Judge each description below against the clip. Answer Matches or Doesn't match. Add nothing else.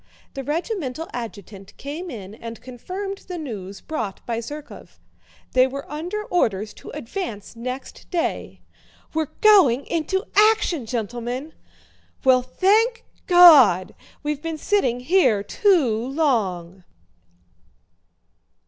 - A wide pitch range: Matches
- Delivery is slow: Matches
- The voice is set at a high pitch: Matches